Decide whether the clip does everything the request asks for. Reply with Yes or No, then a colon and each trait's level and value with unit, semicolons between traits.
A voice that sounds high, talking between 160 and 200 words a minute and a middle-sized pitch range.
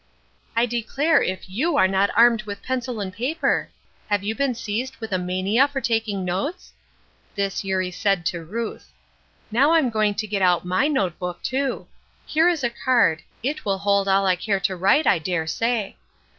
Yes: high, 210 Hz; average, 190 wpm; average, 4.9 semitones